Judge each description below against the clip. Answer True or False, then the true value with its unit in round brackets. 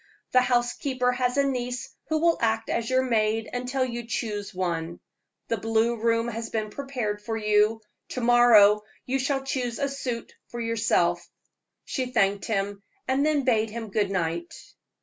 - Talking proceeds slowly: False (165 wpm)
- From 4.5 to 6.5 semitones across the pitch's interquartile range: False (2.9 semitones)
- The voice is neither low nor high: False (230 Hz)